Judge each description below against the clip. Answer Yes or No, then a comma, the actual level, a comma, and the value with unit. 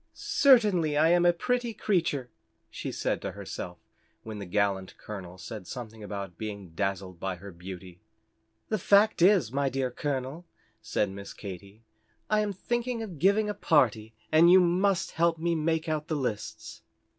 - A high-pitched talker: No, medium, 140 Hz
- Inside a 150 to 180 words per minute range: Yes, average, 165 wpm